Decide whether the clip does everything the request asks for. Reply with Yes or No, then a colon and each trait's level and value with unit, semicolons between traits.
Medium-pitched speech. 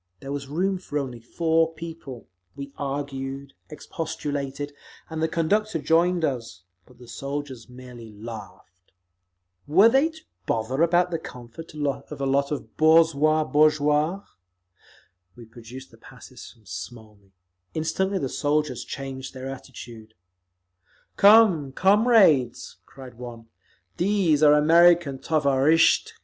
Yes: medium, 145 Hz